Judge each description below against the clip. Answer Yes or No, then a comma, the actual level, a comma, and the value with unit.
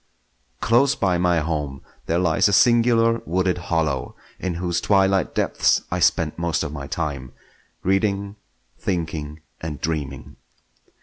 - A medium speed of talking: No, slow, 130 wpm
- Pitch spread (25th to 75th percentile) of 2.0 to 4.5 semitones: Yes, average, 4.1 semitones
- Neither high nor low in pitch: No, very low, 85 Hz